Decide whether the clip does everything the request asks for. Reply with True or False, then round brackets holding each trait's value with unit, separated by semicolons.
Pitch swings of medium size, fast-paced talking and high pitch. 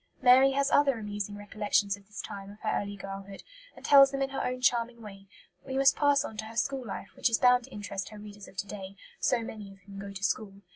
True (4.1 semitones; 255 wpm; 210 Hz)